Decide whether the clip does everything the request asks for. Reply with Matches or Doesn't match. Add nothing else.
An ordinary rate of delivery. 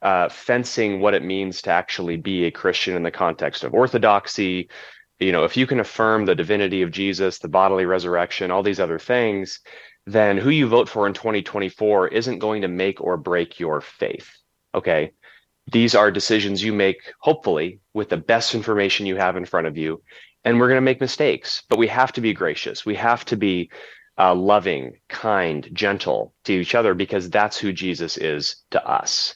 Matches